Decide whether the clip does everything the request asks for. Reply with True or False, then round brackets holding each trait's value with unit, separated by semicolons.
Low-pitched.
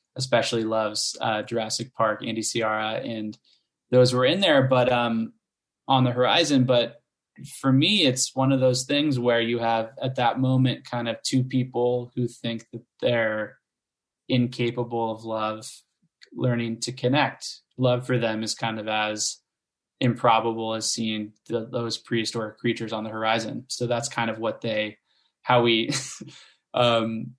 True (120 Hz)